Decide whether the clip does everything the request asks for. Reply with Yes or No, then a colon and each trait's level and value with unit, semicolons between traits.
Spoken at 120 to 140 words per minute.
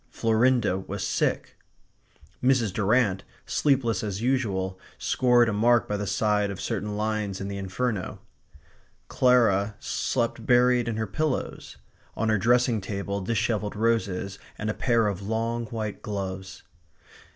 Yes: slow, 135 wpm